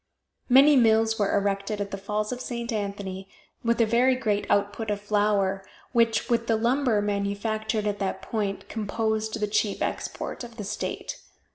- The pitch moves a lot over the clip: No, narrow, 2.4 semitones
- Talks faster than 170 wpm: No, average, 165 wpm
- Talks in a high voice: Yes, high, 215 Hz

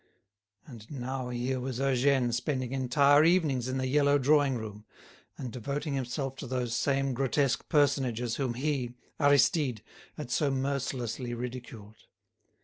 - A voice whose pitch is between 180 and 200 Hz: No, low, 130 Hz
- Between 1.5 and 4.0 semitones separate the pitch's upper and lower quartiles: Yes, narrow, 2.5 semitones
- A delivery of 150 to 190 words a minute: No, slow, 135 wpm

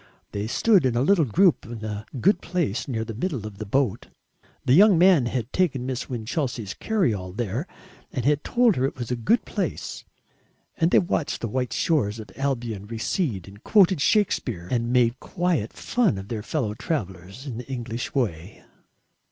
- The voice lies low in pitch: Yes, low, 125 Hz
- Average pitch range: No, wide, 6.7 semitones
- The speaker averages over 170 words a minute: Yes, average, 185 wpm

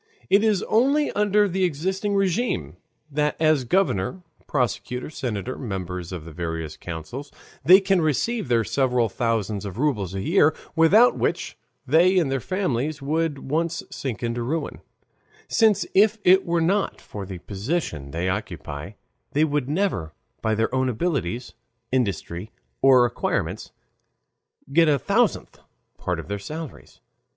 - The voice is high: No, medium, 140 Hz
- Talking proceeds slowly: No, average, 145 wpm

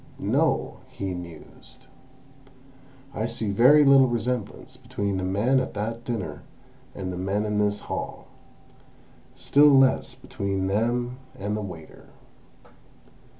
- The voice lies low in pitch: Yes, low, 105 Hz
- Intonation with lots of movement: No, average, 4.2 semitones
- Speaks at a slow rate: Yes, slow, 120 wpm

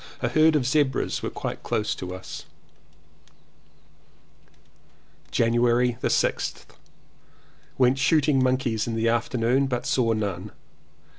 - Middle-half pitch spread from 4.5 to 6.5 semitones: No, average, 2.8 semitones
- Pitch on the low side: Yes, low, 125 Hz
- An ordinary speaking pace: No, slow, 105 wpm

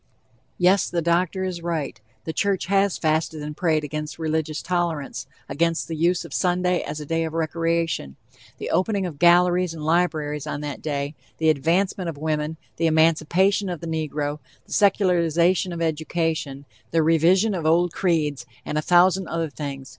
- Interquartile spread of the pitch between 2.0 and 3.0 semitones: Yes, narrow, 2.6 semitones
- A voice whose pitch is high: No, medium, 165 Hz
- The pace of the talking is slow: No, average, 170 wpm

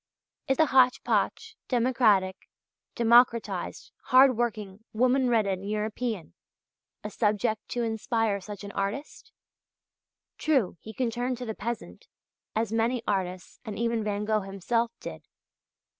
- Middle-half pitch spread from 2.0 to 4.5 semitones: Yes, average, 2.9 semitones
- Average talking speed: No, slow, 130 wpm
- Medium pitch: No, high, 225 Hz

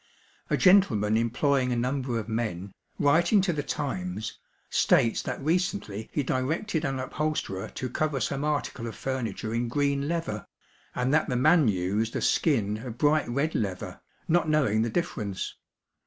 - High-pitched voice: No, low, 130 Hz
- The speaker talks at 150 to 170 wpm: Yes, average, 155 wpm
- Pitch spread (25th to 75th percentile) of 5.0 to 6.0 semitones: Yes, wide, 5.4 semitones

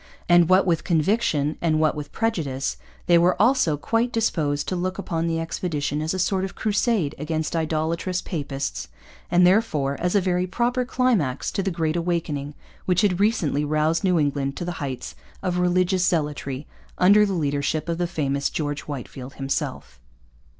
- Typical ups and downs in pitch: Yes, average, 3.9 semitones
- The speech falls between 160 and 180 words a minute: Yes, average, 170 wpm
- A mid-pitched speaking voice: Yes, medium, 170 Hz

